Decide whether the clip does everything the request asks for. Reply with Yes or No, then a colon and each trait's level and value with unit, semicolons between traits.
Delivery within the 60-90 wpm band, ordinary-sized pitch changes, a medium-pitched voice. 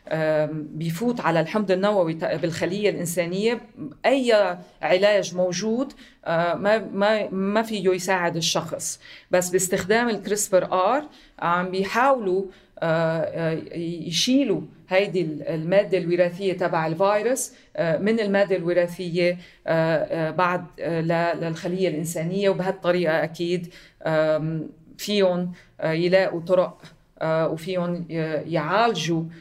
Yes: average, 80 wpm; average, 3.3 semitones; medium, 180 Hz